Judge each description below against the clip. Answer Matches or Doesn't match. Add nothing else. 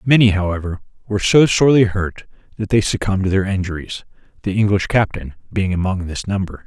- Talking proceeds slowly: Doesn't match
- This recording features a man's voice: Matches